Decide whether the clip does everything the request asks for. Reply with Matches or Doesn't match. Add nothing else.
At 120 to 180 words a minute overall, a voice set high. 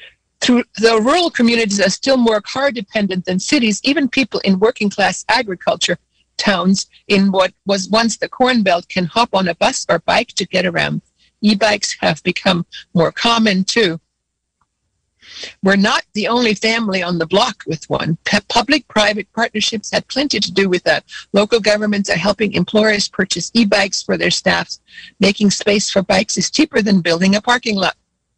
Matches